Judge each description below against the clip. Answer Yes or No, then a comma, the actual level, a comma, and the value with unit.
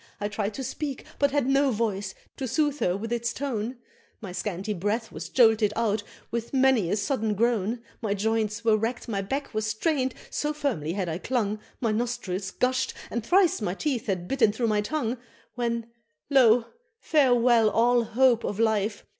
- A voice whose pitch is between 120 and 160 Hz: No, high, 230 Hz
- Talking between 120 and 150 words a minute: No, average, 180 wpm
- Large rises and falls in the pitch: No, average, 3.6 semitones